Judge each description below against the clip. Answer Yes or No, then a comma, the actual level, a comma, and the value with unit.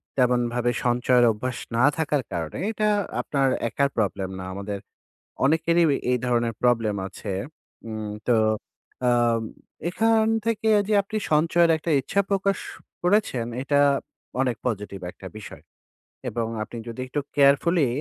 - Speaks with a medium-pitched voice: No, low, 125 Hz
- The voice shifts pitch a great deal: Yes, wide, 6.5 semitones